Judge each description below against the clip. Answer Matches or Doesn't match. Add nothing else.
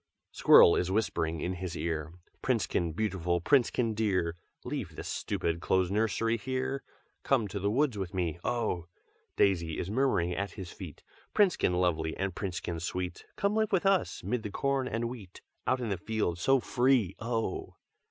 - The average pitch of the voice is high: Doesn't match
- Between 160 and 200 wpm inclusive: Matches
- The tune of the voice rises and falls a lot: Matches